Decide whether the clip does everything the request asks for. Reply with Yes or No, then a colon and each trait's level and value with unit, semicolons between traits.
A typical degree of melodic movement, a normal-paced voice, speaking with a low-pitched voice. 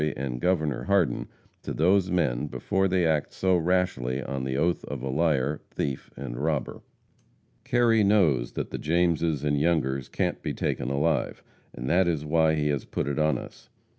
Yes: average, 4.4 semitones; average, 175 wpm; very low, 75 Hz